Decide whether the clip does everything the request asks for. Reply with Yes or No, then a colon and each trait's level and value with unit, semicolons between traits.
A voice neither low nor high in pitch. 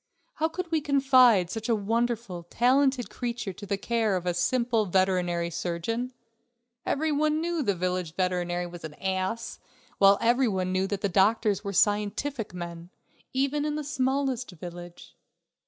No: high, 210 Hz